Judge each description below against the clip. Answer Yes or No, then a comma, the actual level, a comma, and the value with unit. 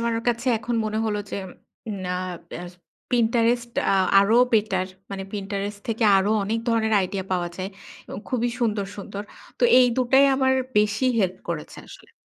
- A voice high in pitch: Yes, high, 215 Hz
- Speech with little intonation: No, average, 3.1 semitones